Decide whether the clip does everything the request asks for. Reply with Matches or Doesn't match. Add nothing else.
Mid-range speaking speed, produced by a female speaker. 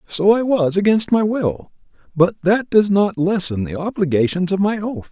Doesn't match